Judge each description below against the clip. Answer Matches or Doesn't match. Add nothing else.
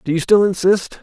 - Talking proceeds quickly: Matches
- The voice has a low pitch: Doesn't match